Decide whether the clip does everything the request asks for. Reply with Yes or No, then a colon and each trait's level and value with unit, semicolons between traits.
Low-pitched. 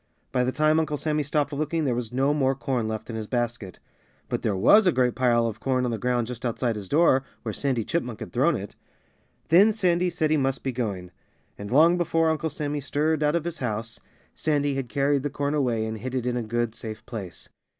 Yes: low, 130 Hz